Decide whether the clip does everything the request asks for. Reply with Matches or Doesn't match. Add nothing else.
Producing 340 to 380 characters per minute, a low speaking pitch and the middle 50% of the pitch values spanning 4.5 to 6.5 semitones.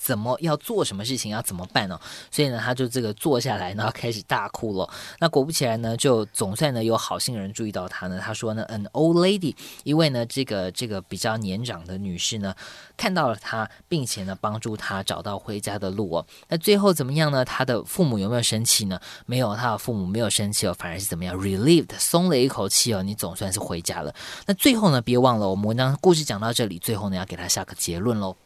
Matches